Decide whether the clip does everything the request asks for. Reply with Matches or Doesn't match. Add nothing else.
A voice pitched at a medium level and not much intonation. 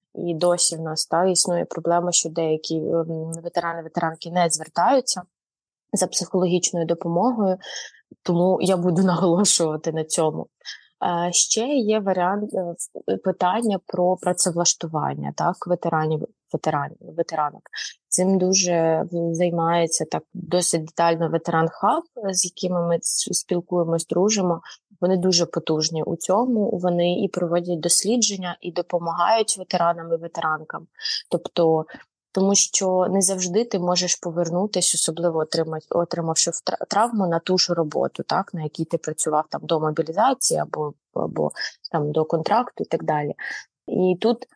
Matches